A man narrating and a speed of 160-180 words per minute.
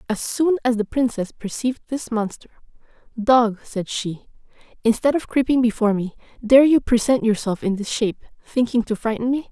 No: female; average, 170 wpm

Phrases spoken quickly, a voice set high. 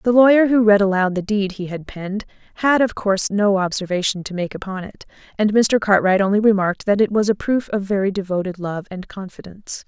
Yes: fast, 215 wpm; high, 200 Hz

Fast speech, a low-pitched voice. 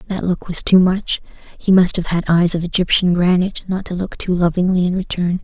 No: fast, 220 wpm; medium, 180 Hz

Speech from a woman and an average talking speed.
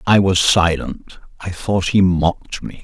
No: male; average, 170 wpm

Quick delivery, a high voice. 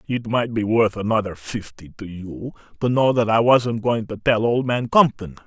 No: fast, 210 wpm; low, 110 Hz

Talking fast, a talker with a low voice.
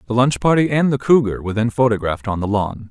Yes: fast, 250 wpm; low, 120 Hz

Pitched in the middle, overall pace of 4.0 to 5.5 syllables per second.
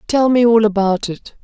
No: high, 220 Hz; 4.8 syllables/s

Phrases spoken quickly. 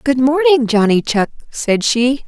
No: average, 160 wpm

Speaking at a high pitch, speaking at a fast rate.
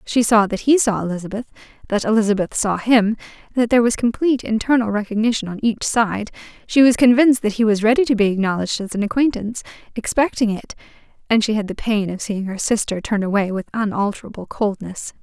No: high, 220 Hz; average, 190 wpm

